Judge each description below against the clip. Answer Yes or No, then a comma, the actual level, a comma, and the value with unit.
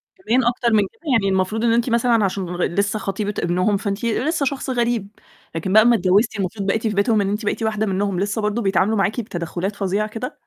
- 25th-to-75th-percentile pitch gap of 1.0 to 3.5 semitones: Yes, average, 2.9 semitones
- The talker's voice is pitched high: Yes, high, 210 Hz